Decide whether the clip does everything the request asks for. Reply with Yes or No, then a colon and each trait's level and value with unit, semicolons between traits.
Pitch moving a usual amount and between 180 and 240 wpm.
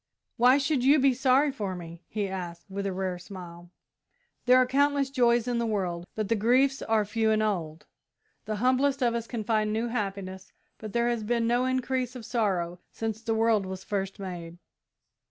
Yes: average, 4.6 semitones; average, 190 wpm